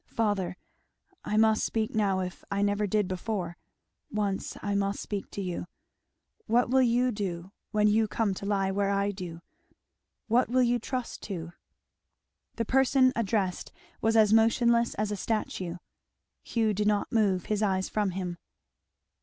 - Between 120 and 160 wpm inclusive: Yes, average, 155 wpm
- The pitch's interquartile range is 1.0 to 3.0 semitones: Yes, average, 2.7 semitones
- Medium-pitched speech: No, high, 210 Hz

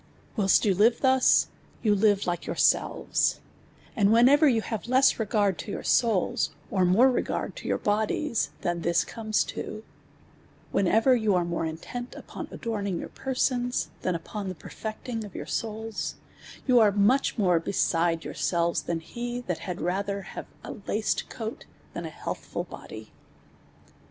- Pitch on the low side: No, high, 210 Hz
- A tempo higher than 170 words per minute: No, average, 155 wpm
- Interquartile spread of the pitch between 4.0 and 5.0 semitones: Yes, average, 4.4 semitones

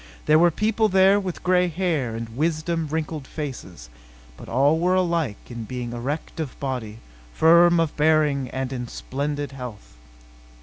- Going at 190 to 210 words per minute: No, average, 150 wpm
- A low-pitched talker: No, medium, 150 Hz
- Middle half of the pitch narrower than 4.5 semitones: No, average, 5.1 semitones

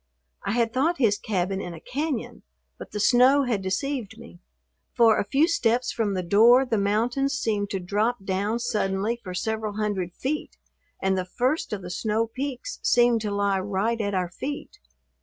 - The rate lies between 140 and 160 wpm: No, average, 180 wpm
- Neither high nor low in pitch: No, high, 220 Hz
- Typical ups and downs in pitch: Yes, average, 3.9 semitones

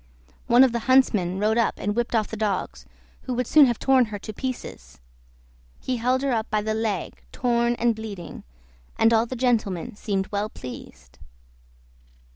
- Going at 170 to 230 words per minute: Yes, average, 175 wpm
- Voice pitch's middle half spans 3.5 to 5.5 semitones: No, average, 2.9 semitones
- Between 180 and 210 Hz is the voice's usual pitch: No, high, 225 Hz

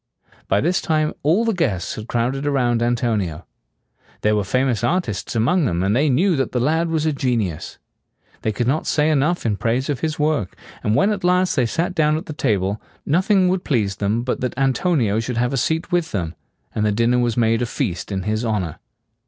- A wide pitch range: Yes, wide, 6.4 semitones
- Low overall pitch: Yes, low, 125 Hz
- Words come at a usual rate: No, fast, 210 wpm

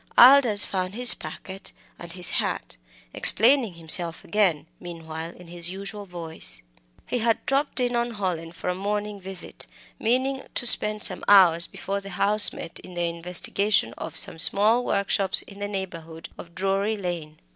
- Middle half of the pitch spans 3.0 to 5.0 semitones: Yes, average, 3.7 semitones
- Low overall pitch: No, high, 195 Hz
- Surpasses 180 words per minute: No, average, 160 wpm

